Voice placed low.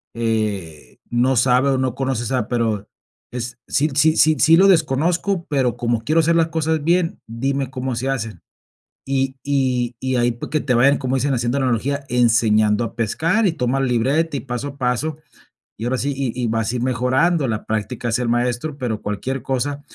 Yes: low, 130 Hz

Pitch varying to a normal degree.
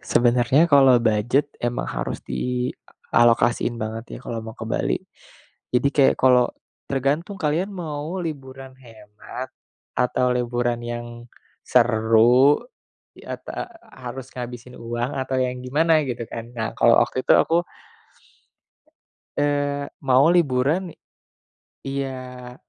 Yes: average, 3.0 semitones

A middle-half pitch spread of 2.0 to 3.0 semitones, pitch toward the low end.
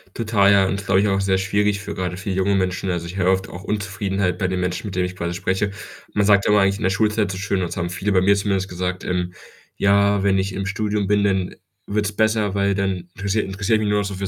No: narrow, 1.6 semitones; very low, 95 Hz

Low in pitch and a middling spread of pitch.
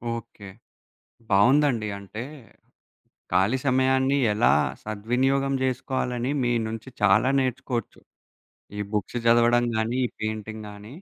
Yes: low, 120 Hz; average, 3.3 semitones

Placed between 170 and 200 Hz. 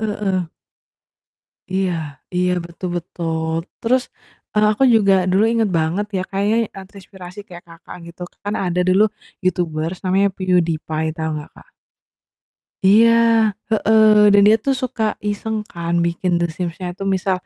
Yes: medium, 185 Hz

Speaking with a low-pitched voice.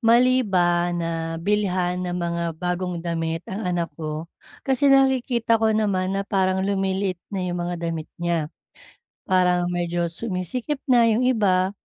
No: medium, 185 Hz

